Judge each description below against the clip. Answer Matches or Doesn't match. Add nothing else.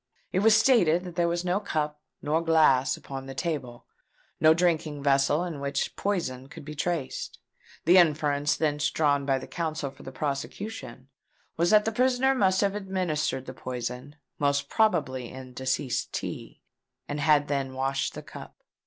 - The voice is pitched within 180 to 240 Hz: Doesn't match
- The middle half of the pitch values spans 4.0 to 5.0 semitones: Matches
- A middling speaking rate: Matches